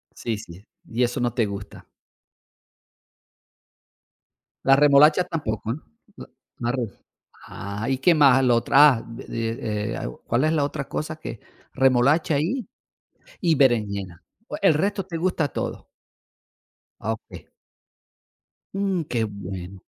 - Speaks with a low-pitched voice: Yes, low, 125 Hz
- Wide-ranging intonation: Yes, wide, 5.9 semitones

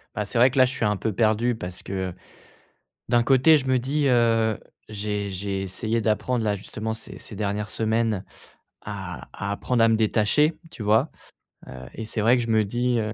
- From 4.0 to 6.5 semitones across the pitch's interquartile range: No, average, 2.7 semitones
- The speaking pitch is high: No, low, 110 Hz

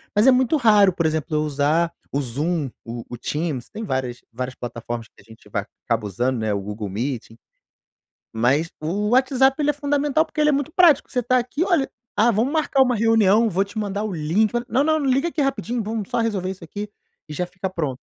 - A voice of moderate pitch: No, high, 195 Hz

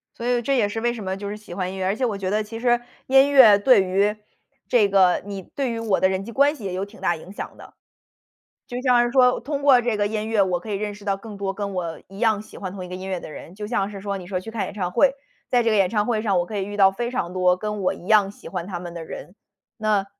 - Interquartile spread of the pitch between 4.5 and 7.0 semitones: No, average, 3.3 semitones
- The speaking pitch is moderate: No, high, 205 Hz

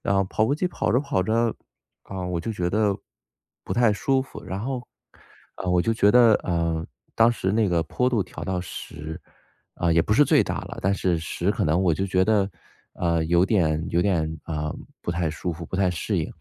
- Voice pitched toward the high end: No, very low, 95 Hz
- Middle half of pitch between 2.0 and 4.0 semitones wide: No, average, 4.6 semitones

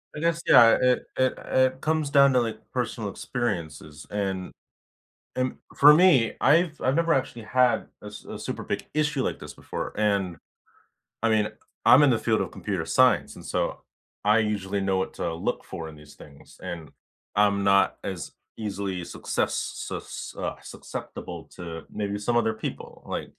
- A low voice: Yes, low, 110 Hz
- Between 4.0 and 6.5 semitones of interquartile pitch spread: Yes, average, 5.1 semitones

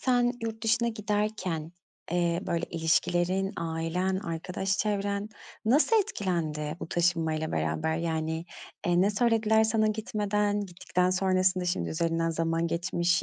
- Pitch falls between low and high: Yes, medium, 180 Hz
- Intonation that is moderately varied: Yes, average, 4.0 semitones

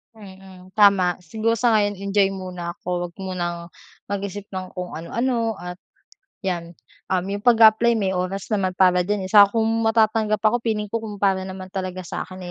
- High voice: Yes, high, 195 Hz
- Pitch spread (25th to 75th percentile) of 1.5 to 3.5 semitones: Yes, average, 2.8 semitones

